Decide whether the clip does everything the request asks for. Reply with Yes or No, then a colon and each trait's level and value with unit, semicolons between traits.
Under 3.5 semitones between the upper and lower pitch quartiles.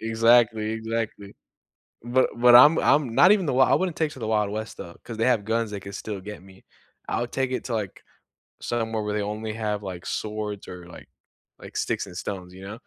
Yes: narrow, 2.6 semitones